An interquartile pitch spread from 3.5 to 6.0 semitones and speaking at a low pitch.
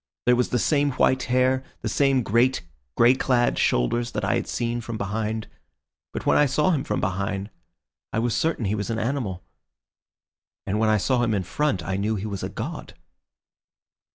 Yes: average, 4.0 semitones; low, 115 Hz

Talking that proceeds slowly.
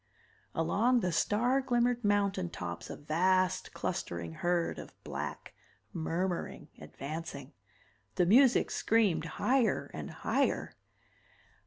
Yes: slow, 105 wpm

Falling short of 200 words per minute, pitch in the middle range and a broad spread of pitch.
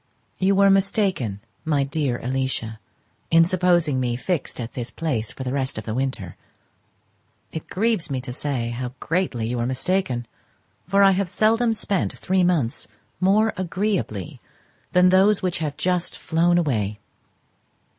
Yes: average, 150 wpm; medium, 160 Hz; wide, 7.0 semitones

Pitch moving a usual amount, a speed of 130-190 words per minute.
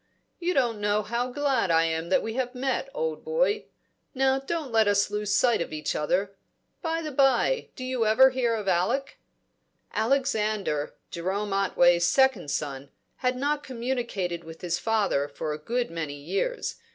No: wide, 7.1 semitones; average, 165 wpm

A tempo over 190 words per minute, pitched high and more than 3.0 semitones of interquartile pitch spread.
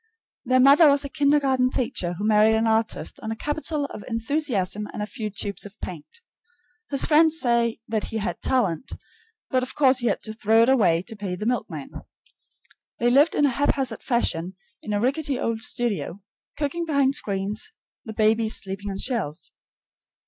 No: average, 180 wpm; high, 230 Hz; average, 4.8 semitones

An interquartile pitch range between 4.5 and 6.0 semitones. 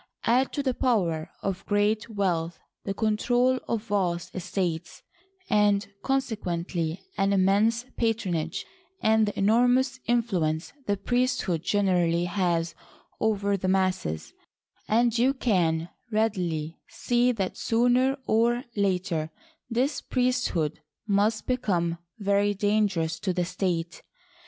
Yes: average, 4.9 semitones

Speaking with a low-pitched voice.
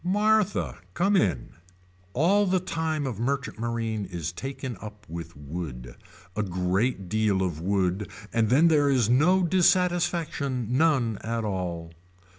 Yes: low, 115 Hz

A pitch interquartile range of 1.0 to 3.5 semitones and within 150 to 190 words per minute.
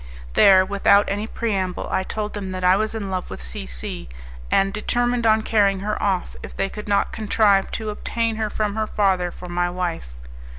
No: narrow, 2.6 semitones; average, 200 wpm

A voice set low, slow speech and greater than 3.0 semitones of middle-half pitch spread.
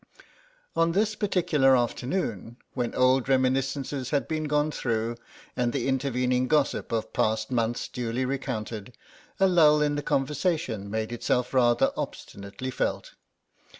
Yes: low, 130 Hz; slow, 130 wpm; average, 3.7 semitones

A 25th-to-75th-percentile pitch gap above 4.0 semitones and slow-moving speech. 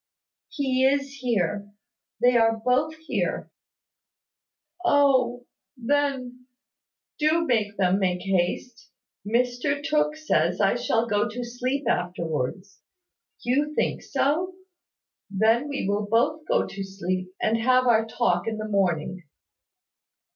Yes: average, 5.3 semitones; slow, 120 wpm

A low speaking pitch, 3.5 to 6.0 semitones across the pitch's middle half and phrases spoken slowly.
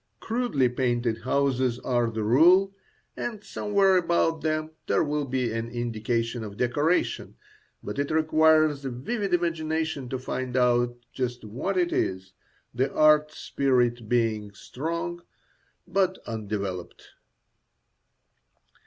Yes: low, 130 Hz; average, 5.0 semitones; slow, 120 wpm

